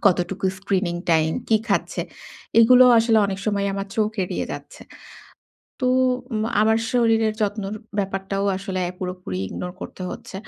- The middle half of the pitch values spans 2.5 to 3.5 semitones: Yes, average, 2.8 semitones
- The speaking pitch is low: No, high, 200 Hz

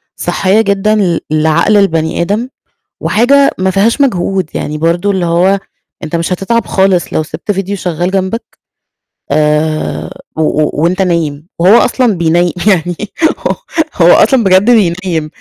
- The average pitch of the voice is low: No, medium, 185 Hz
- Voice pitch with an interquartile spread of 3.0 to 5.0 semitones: Yes, average, 3.4 semitones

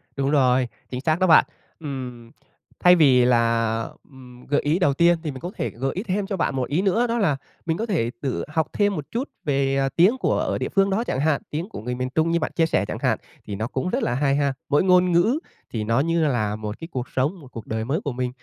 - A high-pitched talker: No, medium, 145 Hz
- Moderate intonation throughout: No, wide, 5.7 semitones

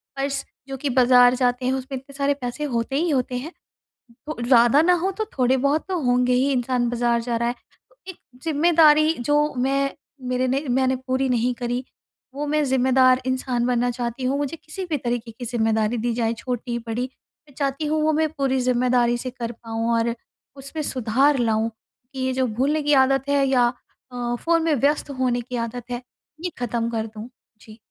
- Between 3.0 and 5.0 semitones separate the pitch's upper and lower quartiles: No, narrow, 2.6 semitones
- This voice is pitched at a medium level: No, very high, 255 Hz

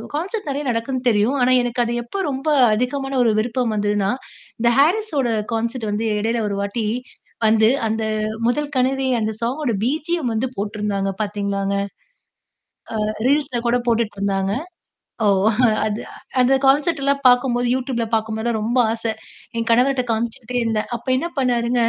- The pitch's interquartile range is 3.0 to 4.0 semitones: Yes, average, 3.5 semitones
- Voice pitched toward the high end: Yes, high, 235 Hz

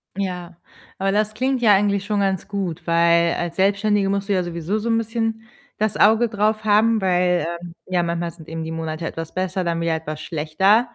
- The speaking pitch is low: No, high, 190 Hz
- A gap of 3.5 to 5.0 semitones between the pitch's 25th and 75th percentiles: Yes, average, 3.9 semitones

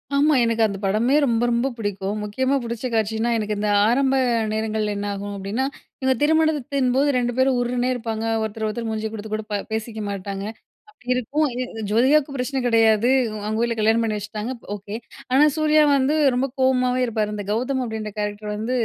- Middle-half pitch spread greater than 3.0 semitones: Yes, average, 3.4 semitones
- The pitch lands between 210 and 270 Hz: Yes, high, 230 Hz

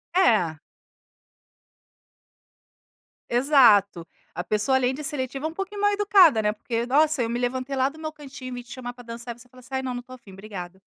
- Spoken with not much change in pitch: No, average, 3.7 semitones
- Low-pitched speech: No, very high, 255 Hz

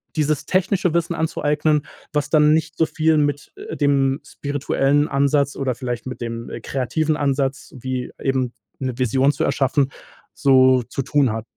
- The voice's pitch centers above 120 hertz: Yes, medium, 140 Hz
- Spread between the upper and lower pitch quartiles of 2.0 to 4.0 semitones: Yes, narrow, 2.6 semitones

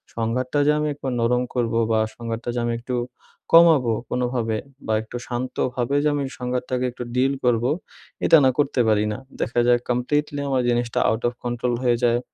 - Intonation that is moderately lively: No, narrow, 1.5 semitones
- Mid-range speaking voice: No, low, 125 Hz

